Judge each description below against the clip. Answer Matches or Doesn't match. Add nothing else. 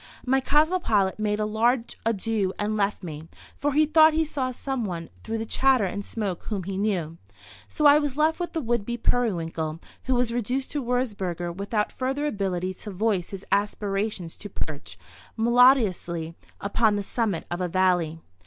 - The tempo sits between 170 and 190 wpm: Matches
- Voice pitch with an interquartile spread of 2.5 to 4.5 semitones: Doesn't match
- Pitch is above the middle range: Matches